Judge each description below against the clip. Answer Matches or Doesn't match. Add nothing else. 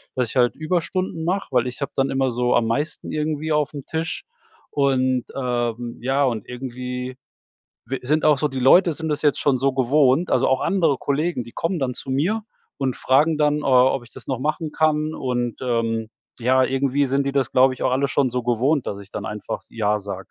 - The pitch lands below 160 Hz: Matches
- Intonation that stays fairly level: Doesn't match